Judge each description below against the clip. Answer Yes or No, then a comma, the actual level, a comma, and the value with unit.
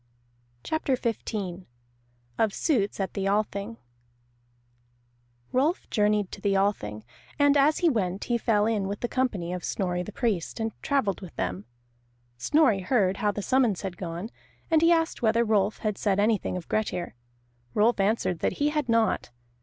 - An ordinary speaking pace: Yes, average, 160 wpm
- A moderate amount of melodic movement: Yes, average, 3.9 semitones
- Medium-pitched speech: No, high, 210 Hz